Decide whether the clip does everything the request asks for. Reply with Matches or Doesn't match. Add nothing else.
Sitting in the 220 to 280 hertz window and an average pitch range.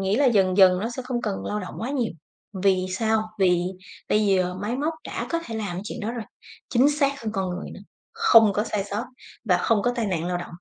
Doesn't match